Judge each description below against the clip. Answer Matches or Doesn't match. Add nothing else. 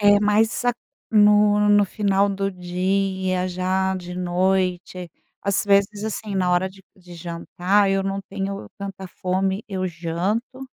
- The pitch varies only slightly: Matches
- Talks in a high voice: Matches